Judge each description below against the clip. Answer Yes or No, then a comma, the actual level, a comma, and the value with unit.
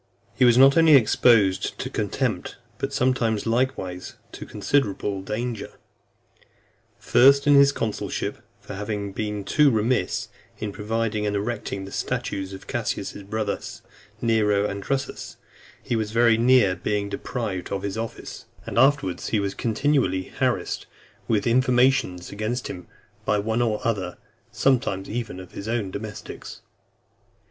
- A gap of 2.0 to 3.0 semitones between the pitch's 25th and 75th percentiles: No, average, 3.5 semitones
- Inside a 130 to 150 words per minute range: Yes, average, 140 wpm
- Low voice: Yes, low, 110 Hz